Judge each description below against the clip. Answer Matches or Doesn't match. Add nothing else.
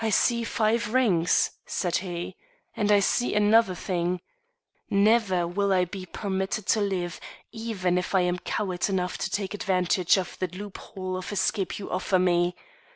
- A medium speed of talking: Matches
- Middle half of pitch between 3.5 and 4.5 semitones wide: Doesn't match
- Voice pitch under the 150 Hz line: Doesn't match